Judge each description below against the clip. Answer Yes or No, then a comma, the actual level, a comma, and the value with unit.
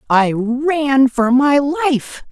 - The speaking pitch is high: Yes, very high, 270 Hz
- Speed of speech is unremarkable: No, slow, 130 wpm